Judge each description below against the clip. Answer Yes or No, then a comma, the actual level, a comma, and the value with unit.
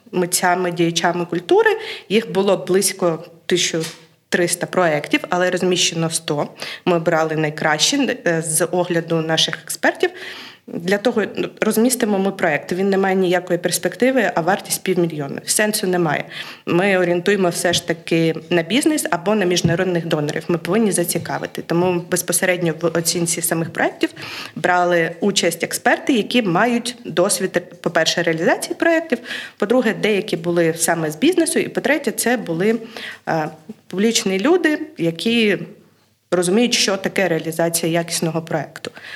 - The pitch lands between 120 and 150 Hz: No, medium, 180 Hz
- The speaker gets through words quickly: No, average, 125 wpm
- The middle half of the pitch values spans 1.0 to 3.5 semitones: No, average, 3.9 semitones